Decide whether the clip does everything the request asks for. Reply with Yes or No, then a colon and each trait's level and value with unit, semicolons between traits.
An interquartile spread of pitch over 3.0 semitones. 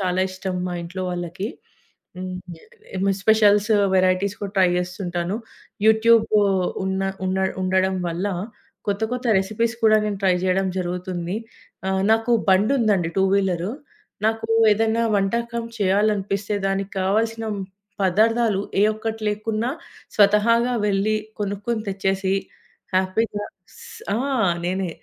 No: average, 2.7 semitones